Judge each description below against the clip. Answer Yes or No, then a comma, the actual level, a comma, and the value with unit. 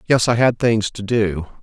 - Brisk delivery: Yes, fast, 220 wpm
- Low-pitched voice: Yes, low, 110 Hz